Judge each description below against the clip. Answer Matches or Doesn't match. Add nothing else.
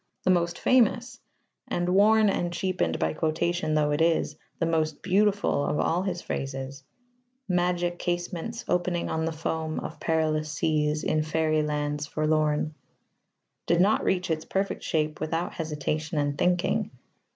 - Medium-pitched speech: Matches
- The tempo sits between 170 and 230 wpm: Doesn't match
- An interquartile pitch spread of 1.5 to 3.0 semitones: Matches